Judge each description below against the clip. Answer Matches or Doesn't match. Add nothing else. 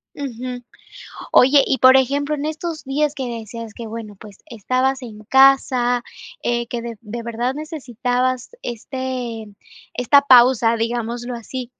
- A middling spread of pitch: Doesn't match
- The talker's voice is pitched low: Doesn't match